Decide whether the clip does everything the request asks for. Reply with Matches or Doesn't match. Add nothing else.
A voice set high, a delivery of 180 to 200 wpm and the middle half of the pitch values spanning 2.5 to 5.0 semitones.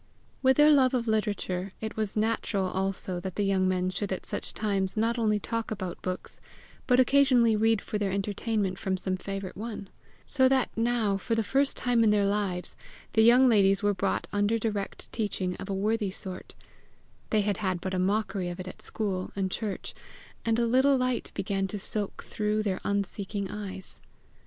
Matches